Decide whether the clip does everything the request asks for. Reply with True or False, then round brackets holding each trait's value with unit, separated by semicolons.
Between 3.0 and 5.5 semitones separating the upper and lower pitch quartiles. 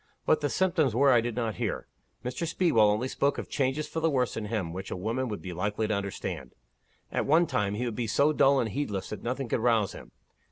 True (5.1 semitones)